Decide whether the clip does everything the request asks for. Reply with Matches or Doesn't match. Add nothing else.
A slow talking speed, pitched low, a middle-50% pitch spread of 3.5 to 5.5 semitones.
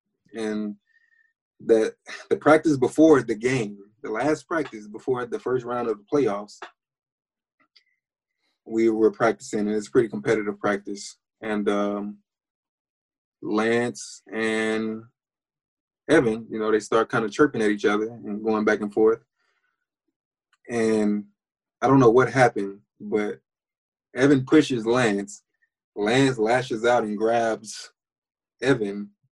Matches